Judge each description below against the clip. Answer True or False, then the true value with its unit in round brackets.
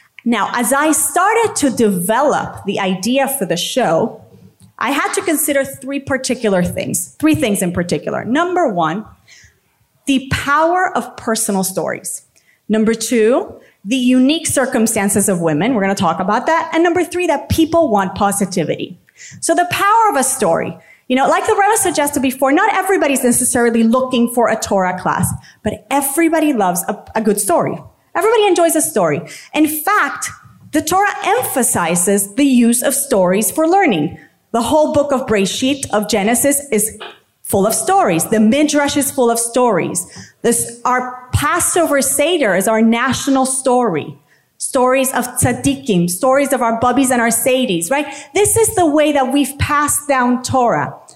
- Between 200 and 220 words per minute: False (160 wpm)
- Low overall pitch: False (260 Hz)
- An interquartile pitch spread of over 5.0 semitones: True (5.4 semitones)